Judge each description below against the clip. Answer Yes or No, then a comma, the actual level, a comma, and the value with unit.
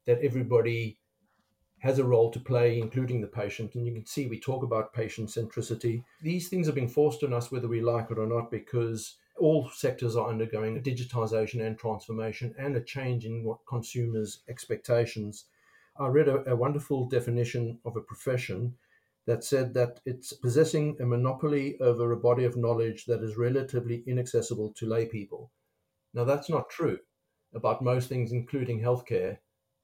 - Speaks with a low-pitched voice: Yes, low, 120 Hz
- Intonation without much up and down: Yes, narrow, 2.3 semitones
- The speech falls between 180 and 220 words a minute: No, average, 170 wpm